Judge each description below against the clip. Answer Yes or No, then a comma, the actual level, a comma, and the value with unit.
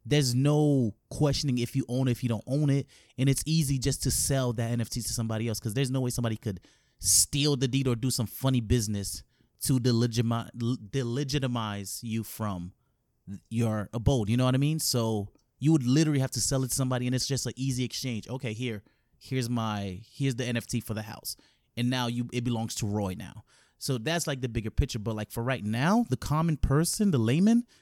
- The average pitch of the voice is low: Yes, low, 125 Hz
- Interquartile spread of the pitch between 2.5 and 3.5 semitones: Yes, average, 3.2 semitones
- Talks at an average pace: No, fast, 210 wpm